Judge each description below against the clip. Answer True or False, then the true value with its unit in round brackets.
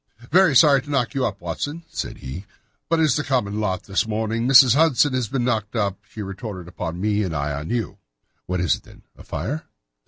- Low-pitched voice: True (110 Hz)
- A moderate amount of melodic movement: False (5.9 semitones)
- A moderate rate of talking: False (210 wpm)